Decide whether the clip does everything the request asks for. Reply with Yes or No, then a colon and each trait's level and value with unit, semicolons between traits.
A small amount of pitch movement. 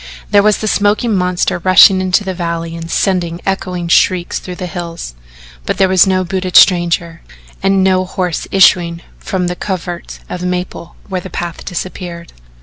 Yes: narrow, 1.6 semitones